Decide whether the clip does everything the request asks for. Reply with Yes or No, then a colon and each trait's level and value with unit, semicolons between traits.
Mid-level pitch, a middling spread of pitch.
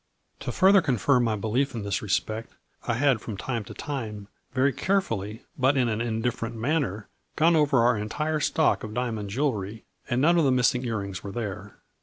No: low, 120 Hz; average, 4.6 semitones